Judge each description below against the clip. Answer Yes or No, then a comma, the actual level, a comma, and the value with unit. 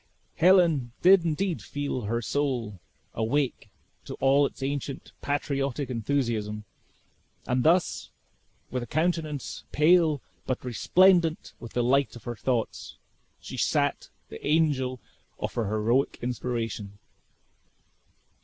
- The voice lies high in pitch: No, low, 135 Hz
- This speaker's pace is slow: Yes, slow, 115 wpm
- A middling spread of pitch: Yes, average, 4.4 semitones